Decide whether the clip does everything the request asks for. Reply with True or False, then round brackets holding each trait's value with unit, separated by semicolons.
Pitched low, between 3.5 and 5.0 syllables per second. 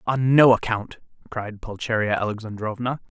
True (115 Hz; 4.9 syllables/s)